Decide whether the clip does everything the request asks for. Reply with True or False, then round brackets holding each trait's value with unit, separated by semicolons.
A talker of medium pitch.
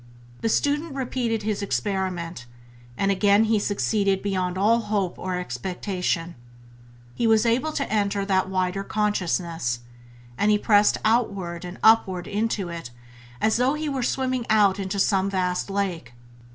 False (200 Hz)